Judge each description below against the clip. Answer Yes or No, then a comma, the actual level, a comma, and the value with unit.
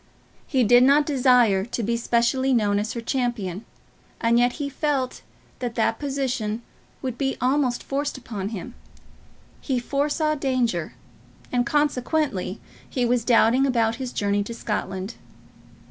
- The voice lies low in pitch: No, high, 245 Hz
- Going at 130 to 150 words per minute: Yes, average, 140 wpm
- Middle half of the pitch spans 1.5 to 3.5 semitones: Yes, average, 3.0 semitones